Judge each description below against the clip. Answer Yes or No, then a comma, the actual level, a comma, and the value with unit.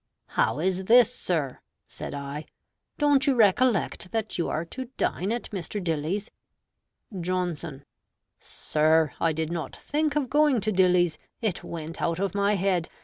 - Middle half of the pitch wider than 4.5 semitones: Yes, wide, 5.5 semitones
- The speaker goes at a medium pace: Yes, average, 150 wpm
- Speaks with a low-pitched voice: No, medium, 185 Hz